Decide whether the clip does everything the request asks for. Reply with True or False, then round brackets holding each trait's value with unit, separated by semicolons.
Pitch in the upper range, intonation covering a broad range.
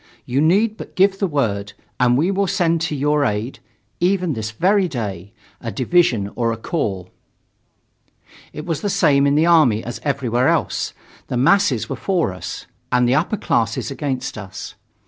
False (140 Hz; 7.2 semitones)